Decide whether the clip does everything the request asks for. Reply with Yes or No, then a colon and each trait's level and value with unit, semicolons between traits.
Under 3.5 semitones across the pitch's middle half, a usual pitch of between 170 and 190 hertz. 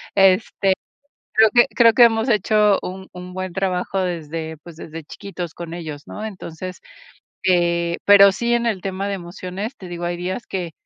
Yes: average, 2.8 semitones; medium, 185 Hz